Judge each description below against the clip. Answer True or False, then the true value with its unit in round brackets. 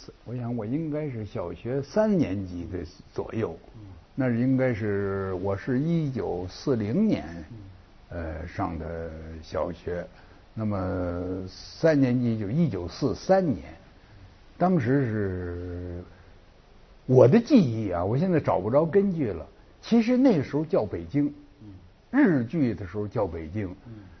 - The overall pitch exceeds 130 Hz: False (105 Hz)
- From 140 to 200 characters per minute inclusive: True (185 characters per minute)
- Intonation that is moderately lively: False (6.8 semitones)